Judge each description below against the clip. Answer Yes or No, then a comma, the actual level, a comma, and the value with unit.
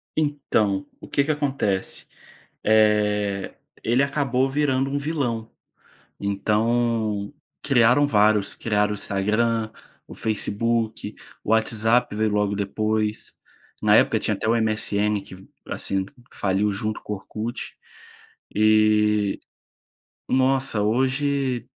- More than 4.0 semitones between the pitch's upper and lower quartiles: No, average, 3.4 semitones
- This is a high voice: No, low, 110 Hz